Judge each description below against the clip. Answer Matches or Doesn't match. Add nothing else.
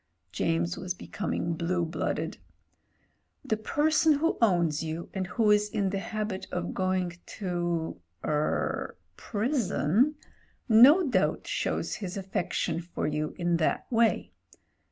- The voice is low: Doesn't match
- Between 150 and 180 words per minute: Doesn't match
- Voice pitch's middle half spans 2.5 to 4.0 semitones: Doesn't match